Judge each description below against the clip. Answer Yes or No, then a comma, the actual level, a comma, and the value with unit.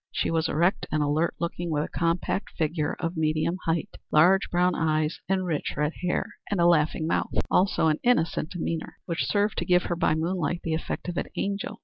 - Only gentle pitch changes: Yes, narrow, 2.2 semitones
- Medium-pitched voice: Yes, medium, 165 Hz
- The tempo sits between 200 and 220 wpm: Yes, fast, 205 wpm